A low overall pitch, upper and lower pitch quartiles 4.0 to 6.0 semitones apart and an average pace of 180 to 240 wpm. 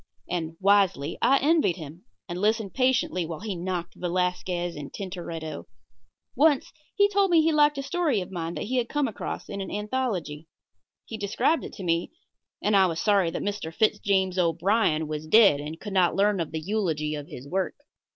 No: high, 190 Hz; average, 4.7 semitones; average, 195 wpm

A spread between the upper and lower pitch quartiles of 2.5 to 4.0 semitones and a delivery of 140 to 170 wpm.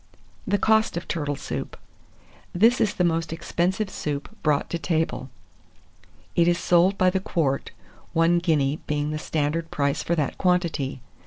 Yes: average, 3.3 semitones; average, 155 wpm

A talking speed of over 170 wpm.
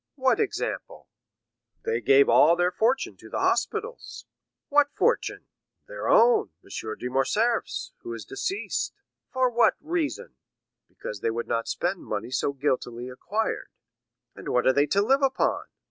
No: average, 145 wpm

